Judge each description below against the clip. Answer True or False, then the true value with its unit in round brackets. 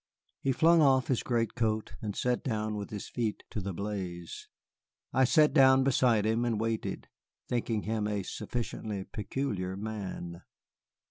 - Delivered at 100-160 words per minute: True (145 wpm)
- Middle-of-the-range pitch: False (110 Hz)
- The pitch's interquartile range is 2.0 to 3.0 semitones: False (3.4 semitones)